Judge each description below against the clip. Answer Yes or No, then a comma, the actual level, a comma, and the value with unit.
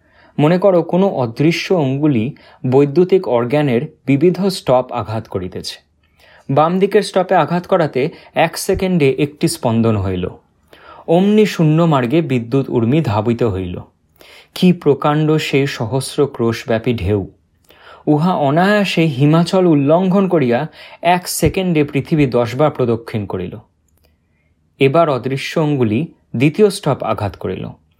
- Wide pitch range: Yes, wide, 6.3 semitones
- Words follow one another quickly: No, average, 110 wpm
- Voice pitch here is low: No, medium, 145 Hz